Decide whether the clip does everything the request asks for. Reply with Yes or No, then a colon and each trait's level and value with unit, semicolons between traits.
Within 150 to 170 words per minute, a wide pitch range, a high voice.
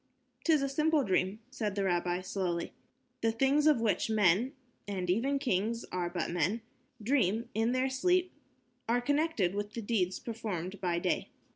Yes: average, 160 wpm; wide, 6.1 semitones; high, 220 Hz